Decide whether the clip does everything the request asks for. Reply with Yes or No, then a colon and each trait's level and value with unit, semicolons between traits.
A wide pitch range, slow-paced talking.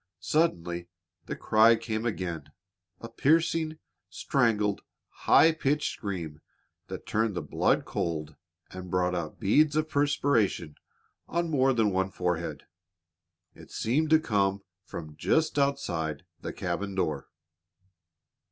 Yes: wide, 8.4 semitones; slow, 120 wpm